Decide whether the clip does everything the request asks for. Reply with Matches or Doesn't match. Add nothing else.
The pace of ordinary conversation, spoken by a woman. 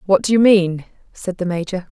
Doesn't match